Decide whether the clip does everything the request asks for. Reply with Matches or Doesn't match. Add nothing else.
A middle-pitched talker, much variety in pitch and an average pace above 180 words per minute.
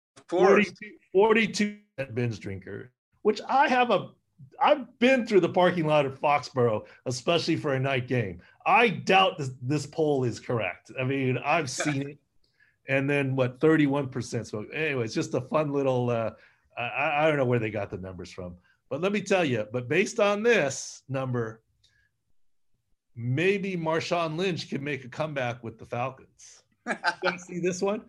Doesn't match